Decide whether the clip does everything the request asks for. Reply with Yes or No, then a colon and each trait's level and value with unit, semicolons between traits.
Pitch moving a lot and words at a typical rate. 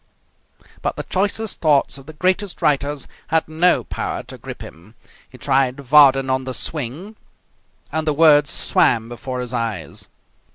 No: average, 3.7 semitones; average, 155 wpm